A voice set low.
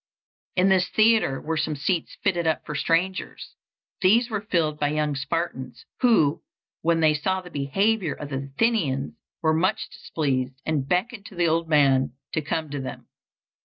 No: medium, 160 Hz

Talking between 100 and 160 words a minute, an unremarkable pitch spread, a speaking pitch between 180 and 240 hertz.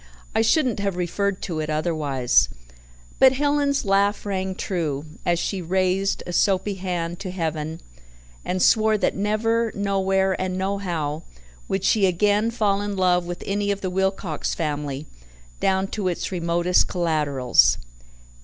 Yes: average, 145 wpm; average, 3.0 semitones; high, 190 Hz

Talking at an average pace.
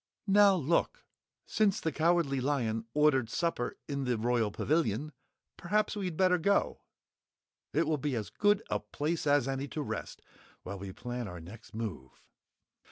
Yes: average, 155 wpm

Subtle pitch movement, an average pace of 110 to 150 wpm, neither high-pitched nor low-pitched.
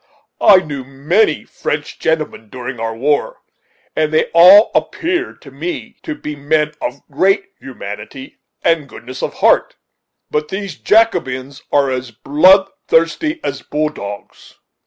No: wide, 5.6 semitones; slow, 135 wpm; medium, 150 Hz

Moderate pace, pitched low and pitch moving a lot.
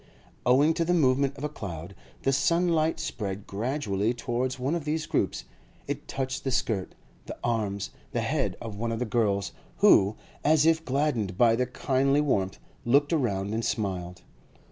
Yes: average, 165 wpm; low, 125 Hz; wide, 6.0 semitones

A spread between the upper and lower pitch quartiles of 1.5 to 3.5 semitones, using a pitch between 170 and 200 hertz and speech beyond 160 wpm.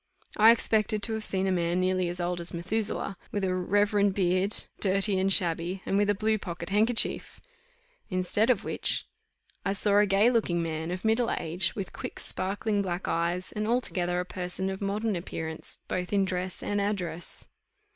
Yes: narrow, 2.6 semitones; high, 190 Hz; average, 180 wpm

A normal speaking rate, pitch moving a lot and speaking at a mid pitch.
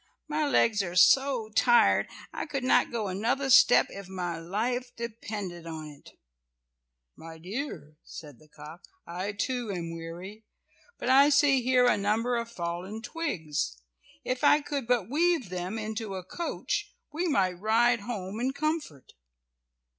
No: average, 150 wpm; wide, 6.3 semitones; high, 220 Hz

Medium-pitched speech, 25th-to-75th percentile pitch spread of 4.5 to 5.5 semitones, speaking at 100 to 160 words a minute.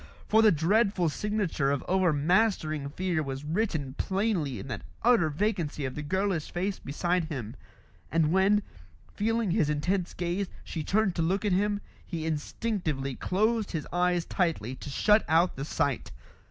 Yes: medium, 175 Hz; average, 5.2 semitones; average, 155 wpm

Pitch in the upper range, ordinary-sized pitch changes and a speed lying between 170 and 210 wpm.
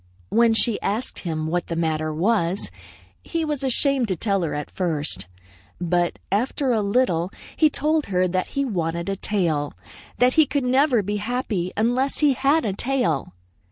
No: high, 205 Hz; wide, 7.1 semitones; average, 175 wpm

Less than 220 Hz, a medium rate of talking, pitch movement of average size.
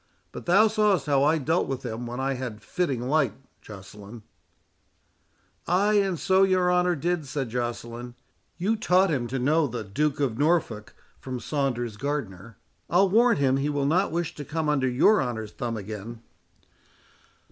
No: medium, 140 Hz; average, 165 wpm; wide, 6.5 semitones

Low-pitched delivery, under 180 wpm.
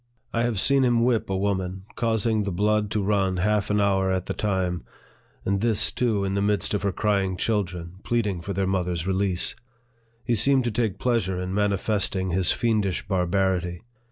No: low, 100 Hz; average, 185 wpm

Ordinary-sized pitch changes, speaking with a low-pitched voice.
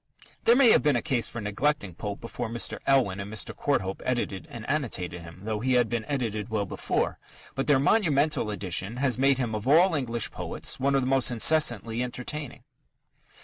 Yes: average, 4.7 semitones; low, 120 Hz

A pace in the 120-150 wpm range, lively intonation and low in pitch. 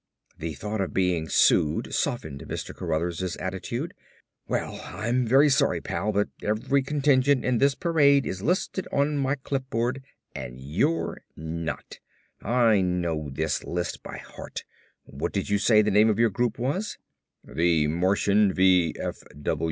Yes: average, 145 wpm; wide, 7.2 semitones; low, 105 Hz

